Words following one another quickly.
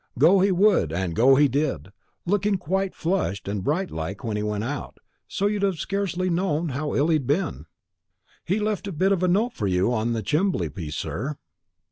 Yes: fast, 210 wpm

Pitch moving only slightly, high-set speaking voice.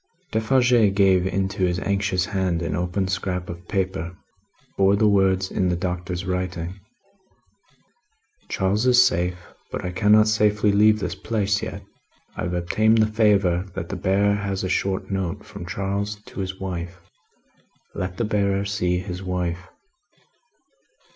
No: narrow, 2.2 semitones; very low, 95 Hz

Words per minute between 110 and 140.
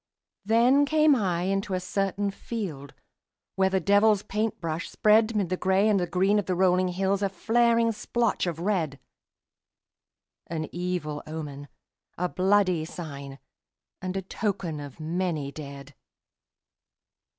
Yes: slow, 135 wpm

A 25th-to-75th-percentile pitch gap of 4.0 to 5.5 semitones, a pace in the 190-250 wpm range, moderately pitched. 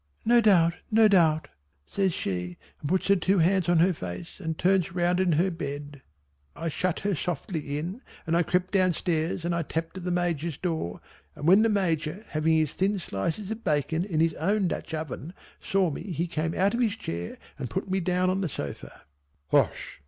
No: average, 3.3 semitones; fast, 205 wpm; medium, 170 Hz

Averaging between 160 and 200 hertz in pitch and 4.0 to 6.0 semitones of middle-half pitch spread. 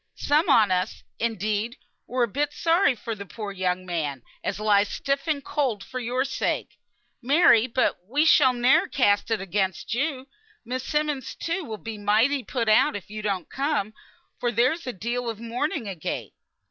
No: high, 235 Hz; average, 5.1 semitones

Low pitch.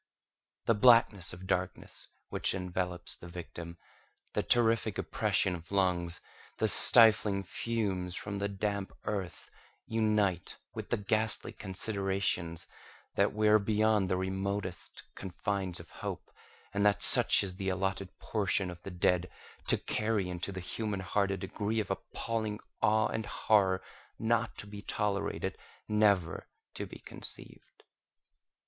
Yes: low, 100 Hz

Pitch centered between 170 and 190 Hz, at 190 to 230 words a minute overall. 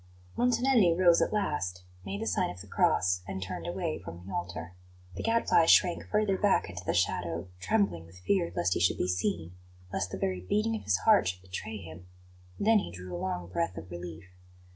No: very low, 90 Hz; fast, 205 wpm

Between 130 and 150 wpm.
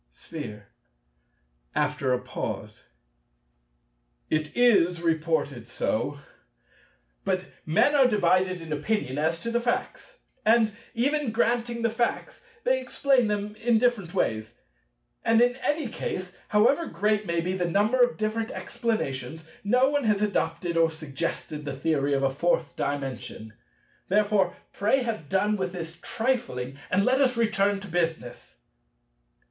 Yes: slow, 135 wpm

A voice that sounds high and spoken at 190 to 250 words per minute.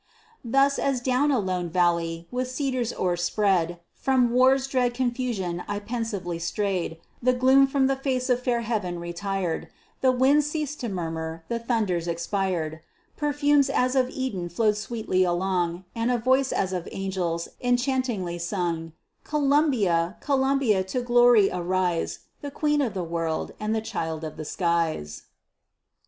No: high, 215 Hz; average, 150 wpm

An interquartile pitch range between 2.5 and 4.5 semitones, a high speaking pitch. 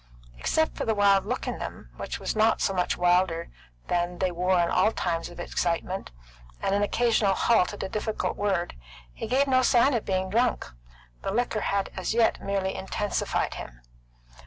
Yes: average, 3.7 semitones; high, 195 Hz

